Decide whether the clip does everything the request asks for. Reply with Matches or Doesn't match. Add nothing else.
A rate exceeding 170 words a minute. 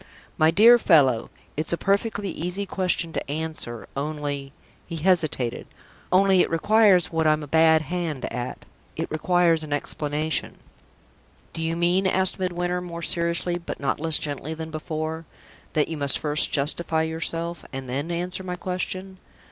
Doesn't match